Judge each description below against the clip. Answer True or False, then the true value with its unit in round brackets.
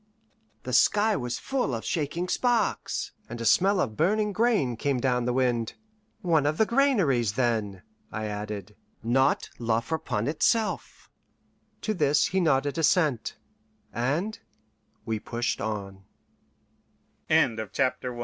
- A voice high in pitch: False (140 Hz)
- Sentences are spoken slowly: True (110 wpm)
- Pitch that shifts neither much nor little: False (8.1 semitones)